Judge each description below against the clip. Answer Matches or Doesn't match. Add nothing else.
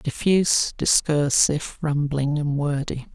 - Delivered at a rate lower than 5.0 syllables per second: Matches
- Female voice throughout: Doesn't match